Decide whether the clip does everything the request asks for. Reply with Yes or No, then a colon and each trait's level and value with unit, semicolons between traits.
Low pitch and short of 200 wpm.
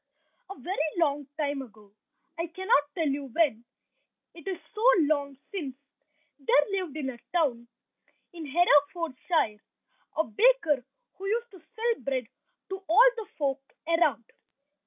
No: very high, 310 Hz; slow, 135 wpm